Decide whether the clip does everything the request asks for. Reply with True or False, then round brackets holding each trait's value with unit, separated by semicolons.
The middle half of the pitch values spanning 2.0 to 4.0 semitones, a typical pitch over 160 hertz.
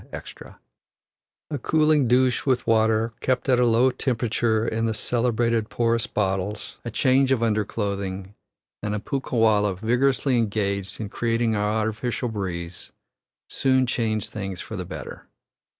False (2.9 semitones; 115 Hz)